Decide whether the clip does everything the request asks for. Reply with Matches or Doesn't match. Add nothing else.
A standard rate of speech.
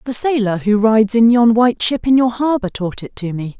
Doesn't match